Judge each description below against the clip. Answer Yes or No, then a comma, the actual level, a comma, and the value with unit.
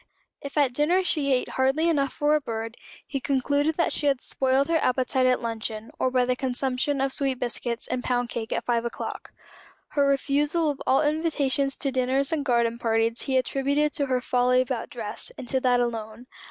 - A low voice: No, very high, 260 Hz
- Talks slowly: No, average, 195 wpm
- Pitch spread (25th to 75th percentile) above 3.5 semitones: No, narrow, 2.5 semitones